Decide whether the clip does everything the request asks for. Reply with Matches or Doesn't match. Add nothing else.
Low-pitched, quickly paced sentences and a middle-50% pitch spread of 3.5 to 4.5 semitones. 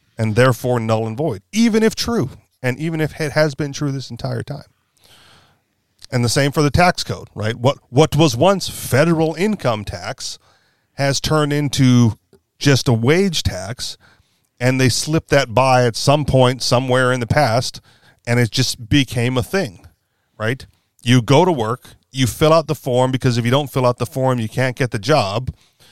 Doesn't match